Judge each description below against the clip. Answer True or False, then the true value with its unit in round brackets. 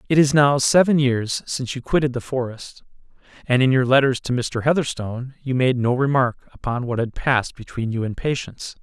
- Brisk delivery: False (195 wpm)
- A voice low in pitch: True (130 Hz)